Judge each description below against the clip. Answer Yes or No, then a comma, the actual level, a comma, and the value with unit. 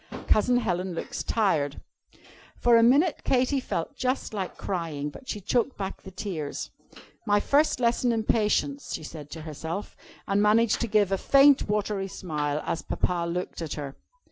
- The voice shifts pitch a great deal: Yes, wide, 6.0 semitones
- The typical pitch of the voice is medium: No, high, 200 Hz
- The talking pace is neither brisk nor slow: Yes, average, 170 wpm